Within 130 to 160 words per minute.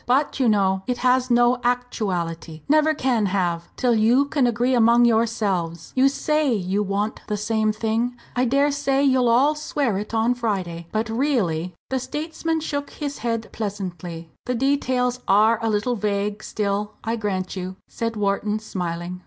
No: average, 170 wpm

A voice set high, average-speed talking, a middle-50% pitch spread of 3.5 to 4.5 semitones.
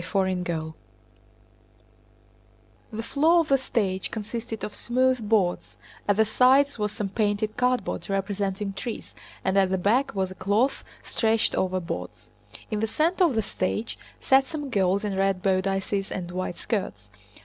Yes: high, 205 Hz; average, 155 wpm; average, 3.9 semitones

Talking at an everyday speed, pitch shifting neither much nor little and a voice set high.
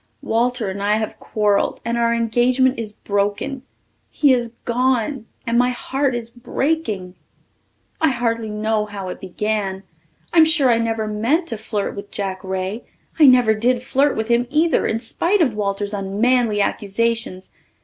Yes: average, 160 wpm; average, 3.4 semitones; high, 230 Hz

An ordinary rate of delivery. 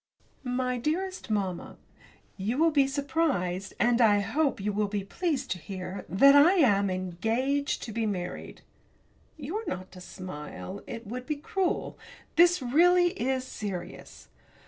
Yes: average, 145 wpm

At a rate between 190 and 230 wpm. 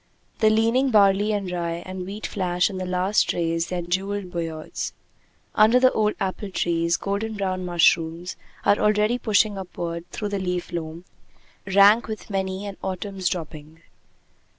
No: average, 150 wpm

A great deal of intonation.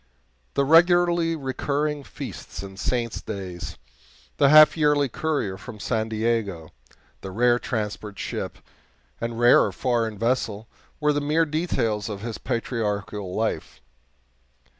Yes: wide, 5.8 semitones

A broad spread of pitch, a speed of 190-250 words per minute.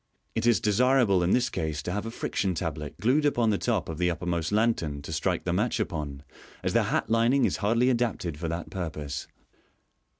Yes: wide, 6.3 semitones; average, 200 wpm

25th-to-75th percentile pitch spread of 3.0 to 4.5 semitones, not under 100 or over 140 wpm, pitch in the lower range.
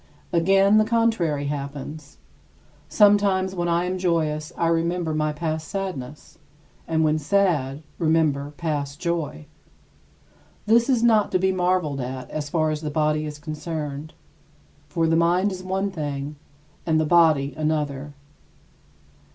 No: average, 3.7 semitones; slow, 135 wpm; medium, 160 Hz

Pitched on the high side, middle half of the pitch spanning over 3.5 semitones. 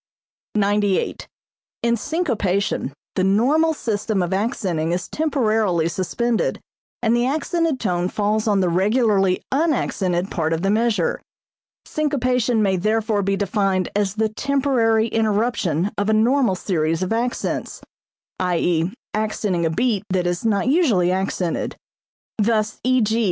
Yes: high, 210 Hz; average, 4.2 semitones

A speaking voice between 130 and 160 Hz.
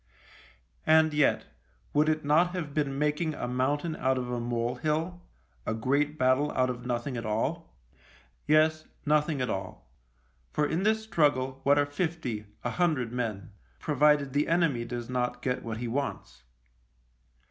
Yes: medium, 140 Hz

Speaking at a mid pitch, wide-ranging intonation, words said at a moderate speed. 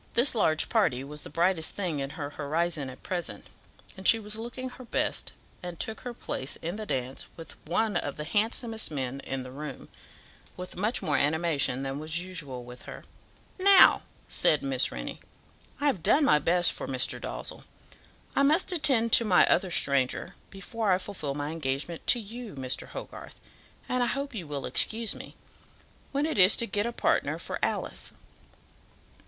Yes: medium, 175 Hz; wide, 7.8 semitones; average, 180 wpm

